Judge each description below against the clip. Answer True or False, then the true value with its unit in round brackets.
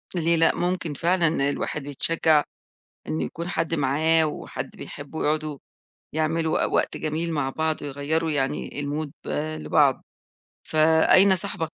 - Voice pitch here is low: False (155 Hz)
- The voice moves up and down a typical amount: False (2.2 semitones)